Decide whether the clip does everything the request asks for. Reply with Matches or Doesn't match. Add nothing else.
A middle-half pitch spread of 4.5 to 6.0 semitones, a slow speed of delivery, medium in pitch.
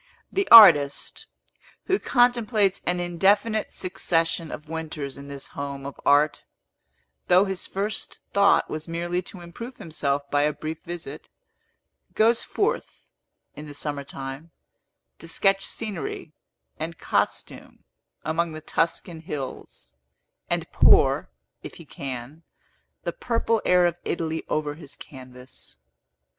Matches